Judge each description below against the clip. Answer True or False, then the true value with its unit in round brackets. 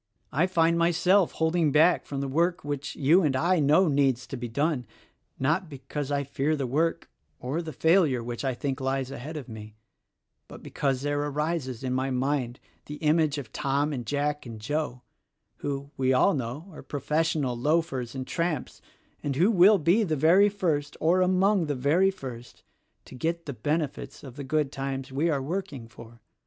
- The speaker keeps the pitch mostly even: False (3.7 semitones)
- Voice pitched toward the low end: False (145 Hz)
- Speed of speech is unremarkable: True (185 wpm)